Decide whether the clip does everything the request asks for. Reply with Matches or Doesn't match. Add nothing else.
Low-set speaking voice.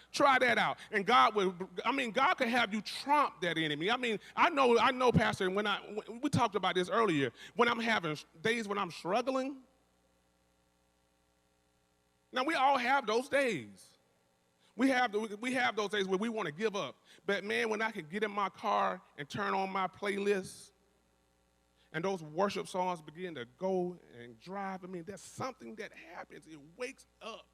Doesn't match